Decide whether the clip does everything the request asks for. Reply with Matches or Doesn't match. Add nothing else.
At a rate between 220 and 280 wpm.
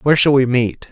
Matches